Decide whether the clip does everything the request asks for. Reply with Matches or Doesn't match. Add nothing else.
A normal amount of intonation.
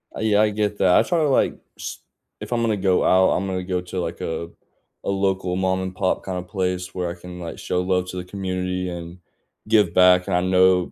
Doesn't match